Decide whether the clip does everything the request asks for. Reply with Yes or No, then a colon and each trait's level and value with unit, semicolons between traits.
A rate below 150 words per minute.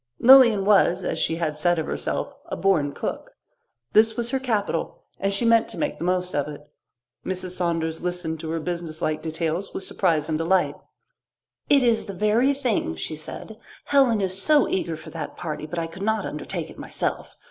No: average, 190 wpm